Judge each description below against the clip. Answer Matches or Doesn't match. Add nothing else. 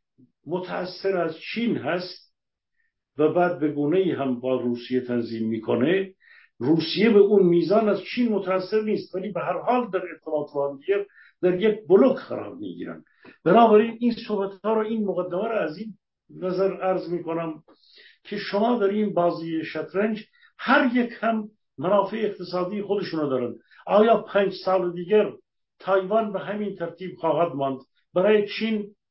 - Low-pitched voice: Doesn't match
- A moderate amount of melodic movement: Matches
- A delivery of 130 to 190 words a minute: Matches